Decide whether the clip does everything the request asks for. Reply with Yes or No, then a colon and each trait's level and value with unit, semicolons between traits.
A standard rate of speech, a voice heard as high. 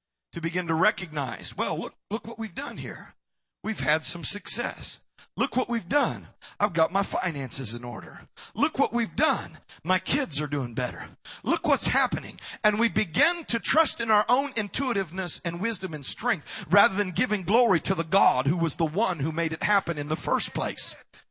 Yes: average, 195 wpm; high, 195 Hz